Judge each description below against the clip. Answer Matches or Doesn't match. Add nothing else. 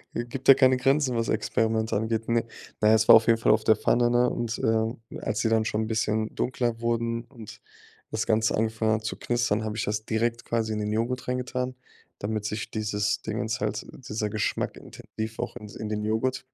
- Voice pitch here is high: Doesn't match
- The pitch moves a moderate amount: Doesn't match